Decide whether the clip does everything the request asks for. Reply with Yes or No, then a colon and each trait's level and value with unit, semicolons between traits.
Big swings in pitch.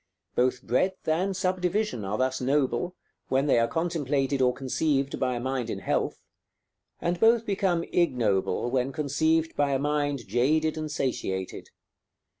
No: average, 4.6 semitones